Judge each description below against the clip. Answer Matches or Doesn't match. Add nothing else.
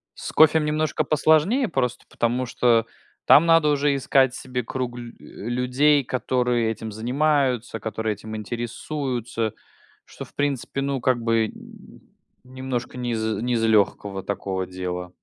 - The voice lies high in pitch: Doesn't match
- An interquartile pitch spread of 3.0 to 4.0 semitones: Matches